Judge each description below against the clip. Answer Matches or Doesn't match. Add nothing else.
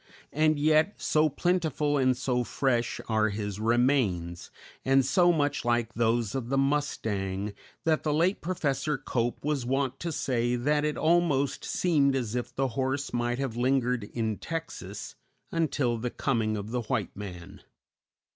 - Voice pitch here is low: Matches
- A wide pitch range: Doesn't match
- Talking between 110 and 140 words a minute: Doesn't match